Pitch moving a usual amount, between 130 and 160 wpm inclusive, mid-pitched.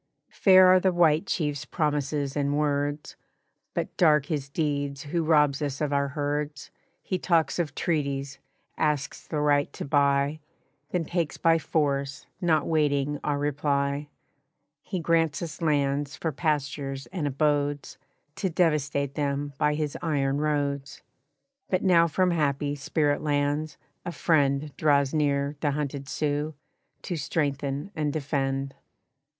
No: narrow, 1.8 semitones; slow, 135 wpm; medium, 145 Hz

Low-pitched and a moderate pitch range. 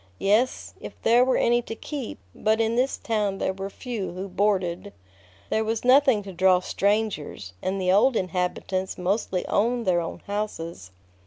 No: high, 205 Hz; average, 3.5 semitones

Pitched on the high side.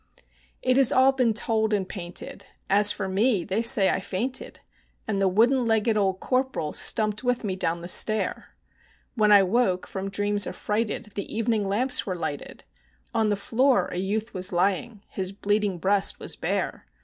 Yes: high, 210 Hz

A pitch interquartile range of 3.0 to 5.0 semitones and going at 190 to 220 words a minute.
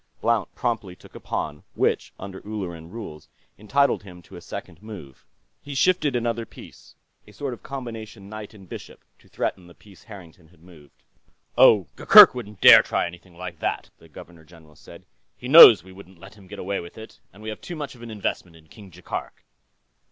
Yes: average, 4.5 semitones; average, 195 wpm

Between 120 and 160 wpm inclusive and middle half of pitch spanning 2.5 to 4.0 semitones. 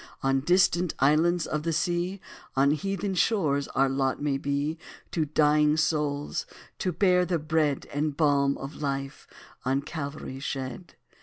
Yes: average, 145 wpm; average, 3.6 semitones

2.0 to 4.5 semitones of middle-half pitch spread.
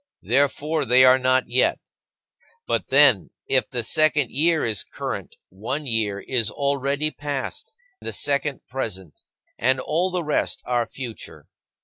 Yes: average, 3.5 semitones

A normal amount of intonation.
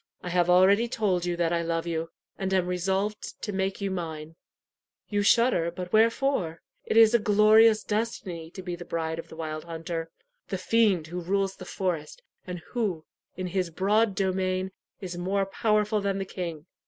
Yes: average, 3.3 semitones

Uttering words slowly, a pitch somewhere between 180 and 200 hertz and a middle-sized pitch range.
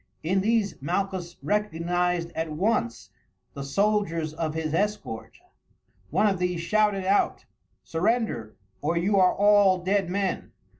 Yes: slow, 130 wpm; medium, 185 Hz; average, 3.6 semitones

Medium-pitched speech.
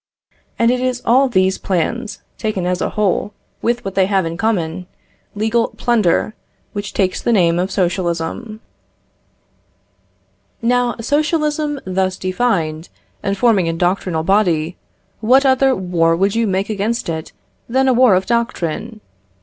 No: high, 200 Hz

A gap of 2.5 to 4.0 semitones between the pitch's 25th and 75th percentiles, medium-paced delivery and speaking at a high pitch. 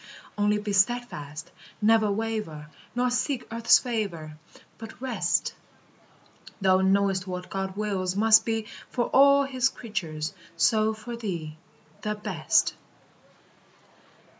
No: average, 3.6 semitones; slow, 115 wpm; high, 210 Hz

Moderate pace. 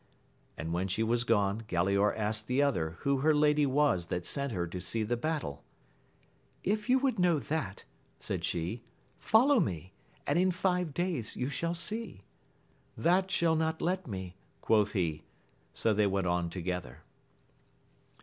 Yes: average, 160 wpm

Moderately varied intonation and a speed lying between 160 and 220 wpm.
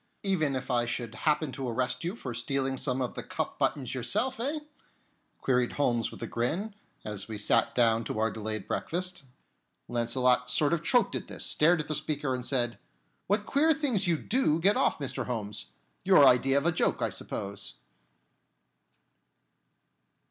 No: wide, 6.0 semitones; average, 170 wpm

